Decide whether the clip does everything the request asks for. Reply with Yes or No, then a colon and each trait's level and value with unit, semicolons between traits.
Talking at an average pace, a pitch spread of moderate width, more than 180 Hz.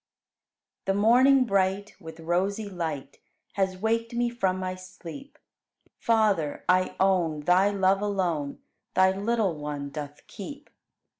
No: slow, 130 wpm; average, 3.8 semitones; high, 190 Hz